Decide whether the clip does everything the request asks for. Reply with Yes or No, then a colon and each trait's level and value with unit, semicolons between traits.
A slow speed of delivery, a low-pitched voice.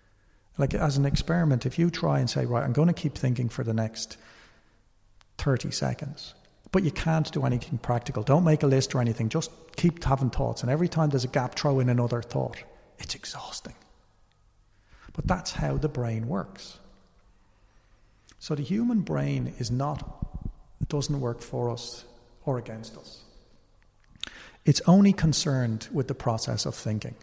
No: average, 165 wpm; low, 125 Hz